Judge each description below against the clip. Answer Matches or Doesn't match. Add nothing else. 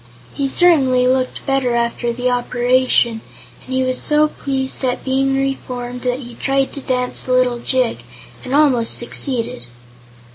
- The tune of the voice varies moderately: Doesn't match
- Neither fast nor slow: Matches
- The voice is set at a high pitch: Matches